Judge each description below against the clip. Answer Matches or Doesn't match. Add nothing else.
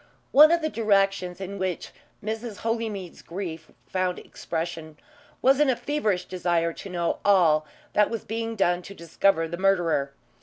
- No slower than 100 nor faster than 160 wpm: Matches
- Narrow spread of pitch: Doesn't match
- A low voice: Doesn't match